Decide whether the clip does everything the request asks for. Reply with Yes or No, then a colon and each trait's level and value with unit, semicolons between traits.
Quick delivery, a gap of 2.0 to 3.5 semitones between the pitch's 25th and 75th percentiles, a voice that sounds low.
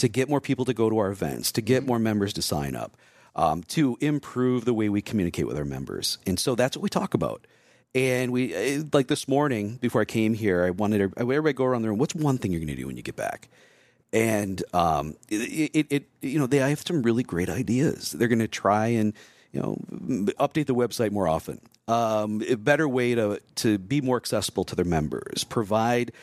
No: fast, 225 wpm; average, 4.4 semitones; low, 120 Hz